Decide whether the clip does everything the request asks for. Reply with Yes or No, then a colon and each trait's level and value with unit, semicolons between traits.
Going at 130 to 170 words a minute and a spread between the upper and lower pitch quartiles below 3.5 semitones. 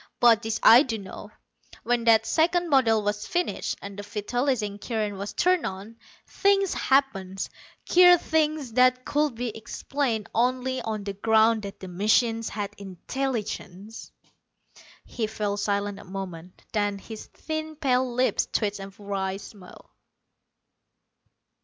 No: average, 140 wpm; average, 4.3 semitones